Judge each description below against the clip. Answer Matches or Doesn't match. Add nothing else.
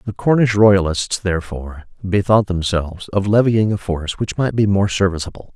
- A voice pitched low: Matches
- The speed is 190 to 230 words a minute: Doesn't match